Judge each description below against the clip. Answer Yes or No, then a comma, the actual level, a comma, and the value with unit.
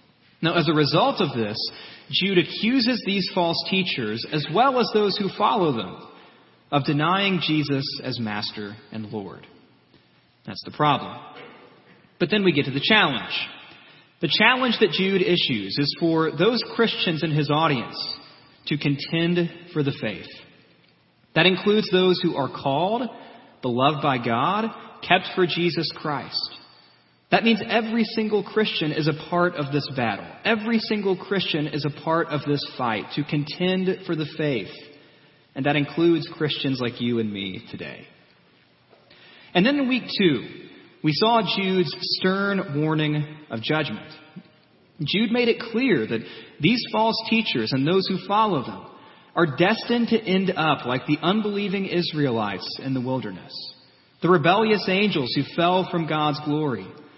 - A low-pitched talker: No, medium, 165 Hz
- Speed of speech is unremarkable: Yes, average, 150 wpm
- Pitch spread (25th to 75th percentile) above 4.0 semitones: Yes, average, 5.1 semitones